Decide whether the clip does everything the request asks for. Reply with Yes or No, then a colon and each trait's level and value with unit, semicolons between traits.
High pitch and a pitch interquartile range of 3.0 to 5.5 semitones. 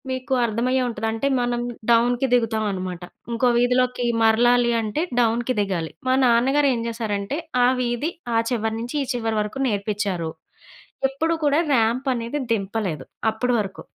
No: high, 235 Hz; narrow, 2.6 semitones